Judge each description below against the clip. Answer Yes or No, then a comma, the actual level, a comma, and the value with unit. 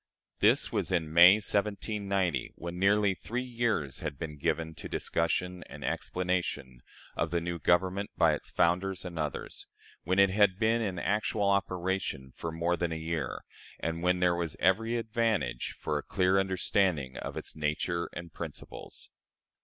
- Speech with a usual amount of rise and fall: Yes, average, 3.2 semitones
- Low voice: Yes, very low, 90 Hz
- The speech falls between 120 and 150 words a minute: No, average, 160 wpm